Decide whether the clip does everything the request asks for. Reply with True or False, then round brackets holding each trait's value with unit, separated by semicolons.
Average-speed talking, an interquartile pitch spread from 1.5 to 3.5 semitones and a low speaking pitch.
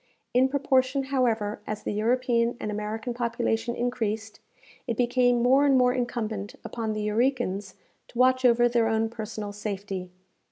False (150 wpm; 2.8 semitones; 235 Hz)